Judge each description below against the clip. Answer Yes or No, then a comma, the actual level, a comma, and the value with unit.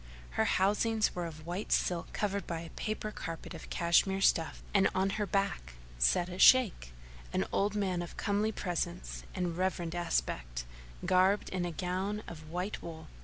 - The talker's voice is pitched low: No, medium, 180 Hz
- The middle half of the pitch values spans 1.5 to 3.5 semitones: Yes, average, 3.0 semitones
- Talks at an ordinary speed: Yes, average, 170 wpm